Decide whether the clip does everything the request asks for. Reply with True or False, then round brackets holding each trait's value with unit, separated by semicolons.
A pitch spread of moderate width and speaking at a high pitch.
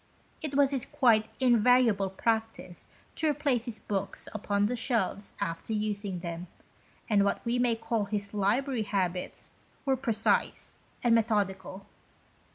True (3.6 semitones; 220 Hz)